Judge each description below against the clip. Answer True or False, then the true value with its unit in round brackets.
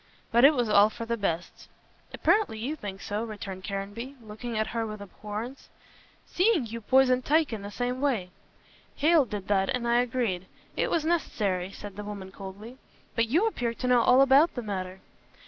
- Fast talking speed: False (185 wpm)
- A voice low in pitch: False (230 Hz)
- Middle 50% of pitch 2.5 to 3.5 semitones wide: False (4.0 semitones)